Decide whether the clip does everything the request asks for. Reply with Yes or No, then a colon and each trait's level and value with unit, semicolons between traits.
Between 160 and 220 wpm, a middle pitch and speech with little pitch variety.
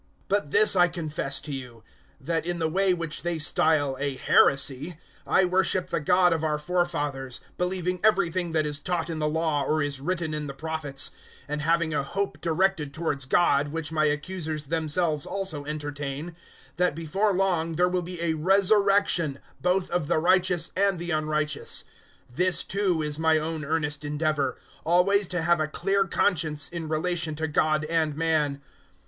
No: average, 175 wpm; medium, 160 Hz; average, 3.1 semitones